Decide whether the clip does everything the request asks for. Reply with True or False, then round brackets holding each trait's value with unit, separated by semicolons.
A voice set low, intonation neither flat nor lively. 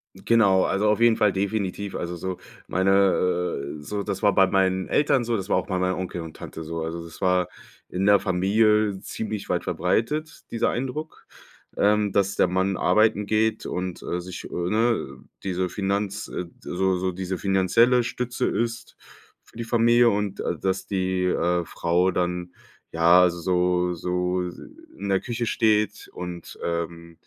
True (95 Hz; 3.2 semitones)